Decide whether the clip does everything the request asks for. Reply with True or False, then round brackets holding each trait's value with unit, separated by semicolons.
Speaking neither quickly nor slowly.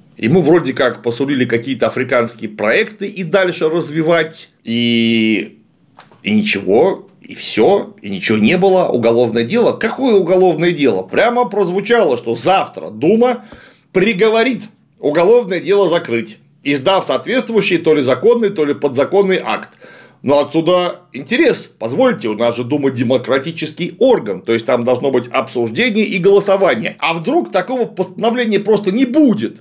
True (135 wpm)